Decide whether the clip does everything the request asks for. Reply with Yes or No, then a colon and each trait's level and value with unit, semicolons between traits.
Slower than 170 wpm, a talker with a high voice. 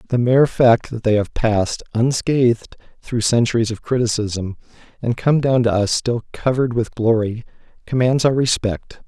No: average, 160 wpm; low, 115 Hz